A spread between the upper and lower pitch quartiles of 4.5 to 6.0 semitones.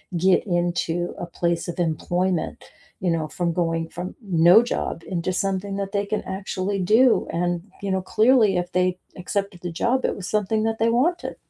No: average, 2.7 semitones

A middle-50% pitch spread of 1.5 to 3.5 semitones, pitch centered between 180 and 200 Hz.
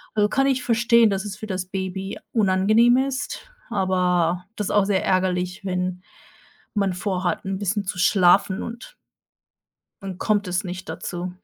Yes: average, 2.7 semitones; high, 190 Hz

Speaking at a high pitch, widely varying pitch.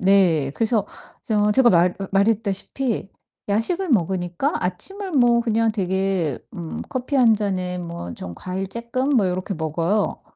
No: high, 200 Hz; average, 4.5 semitones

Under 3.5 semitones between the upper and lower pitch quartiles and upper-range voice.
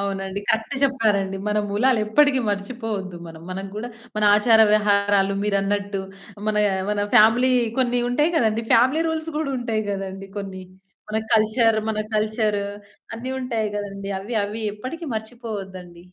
Yes: average, 3.1 semitones; high, 215 Hz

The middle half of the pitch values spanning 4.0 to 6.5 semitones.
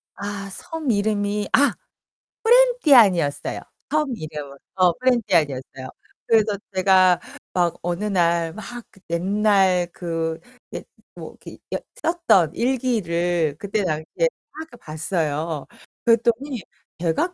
Yes: wide, 5.5 semitones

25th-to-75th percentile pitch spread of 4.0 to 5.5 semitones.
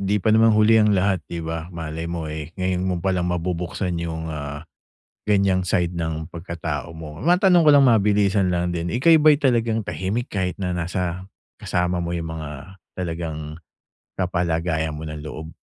No: average, 3.3 semitones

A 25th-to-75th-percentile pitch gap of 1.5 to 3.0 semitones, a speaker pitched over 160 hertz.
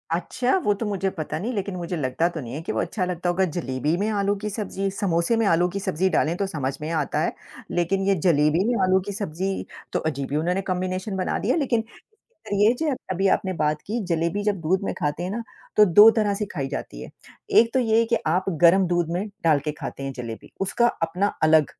No: average, 4.0 semitones; medium, 185 Hz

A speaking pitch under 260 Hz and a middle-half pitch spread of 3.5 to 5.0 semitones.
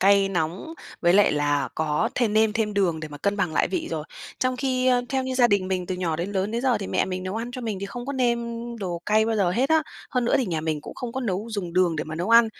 No: high, 200 Hz; wide, 5.4 semitones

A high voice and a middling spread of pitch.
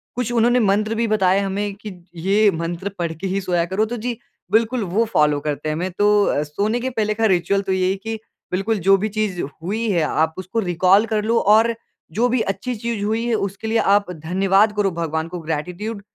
Yes: high, 200 Hz; average, 3.6 semitones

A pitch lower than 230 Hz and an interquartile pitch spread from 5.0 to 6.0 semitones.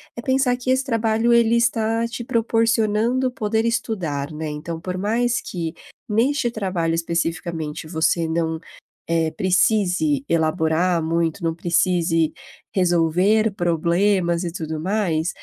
Yes: medium, 185 Hz; wide, 5.5 semitones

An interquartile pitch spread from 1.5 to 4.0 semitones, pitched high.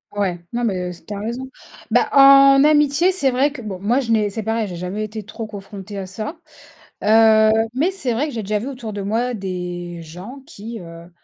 No: average, 5.0 semitones; high, 220 Hz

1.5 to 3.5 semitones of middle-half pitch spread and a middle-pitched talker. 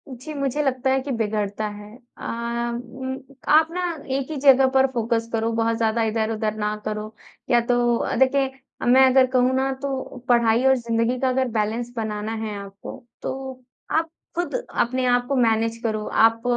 No: average, 2.9 semitones; high, 240 Hz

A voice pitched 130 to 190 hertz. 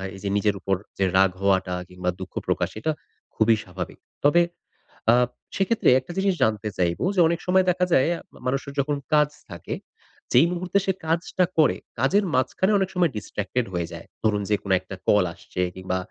No: low, 115 Hz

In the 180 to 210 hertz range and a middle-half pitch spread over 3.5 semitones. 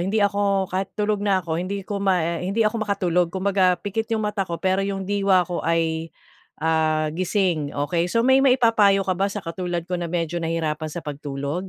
No: medium, 185 Hz; average, 3.2 semitones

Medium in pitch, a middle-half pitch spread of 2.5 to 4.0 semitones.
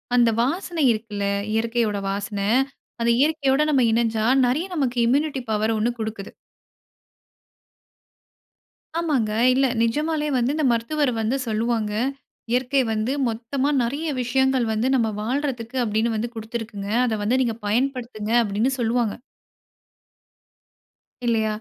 No: high, 235 Hz; average, 3.5 semitones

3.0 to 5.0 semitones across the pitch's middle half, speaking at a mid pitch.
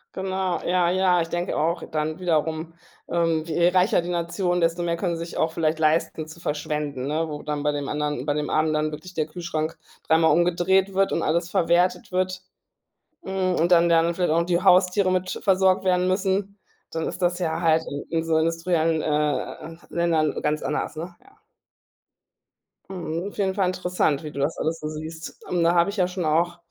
No: narrow, 2.5 semitones; medium, 170 Hz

